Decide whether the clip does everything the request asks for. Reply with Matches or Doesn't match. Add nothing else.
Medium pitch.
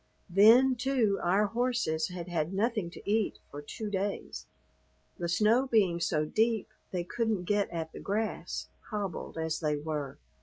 Doesn't match